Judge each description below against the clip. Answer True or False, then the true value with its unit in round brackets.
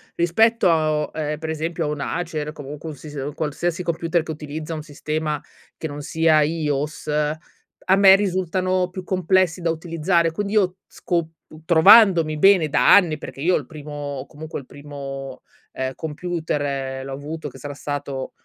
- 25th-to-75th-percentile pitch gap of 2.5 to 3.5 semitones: True (2.9 semitones)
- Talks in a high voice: False (160 Hz)